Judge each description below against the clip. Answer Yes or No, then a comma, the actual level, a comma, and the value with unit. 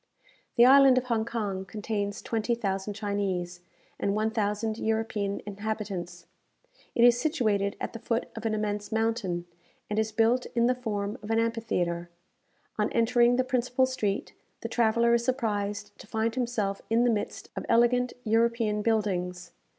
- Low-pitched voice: No, high, 220 Hz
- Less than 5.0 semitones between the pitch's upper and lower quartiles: Yes, narrow, 2.5 semitones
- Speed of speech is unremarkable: Yes, average, 160 wpm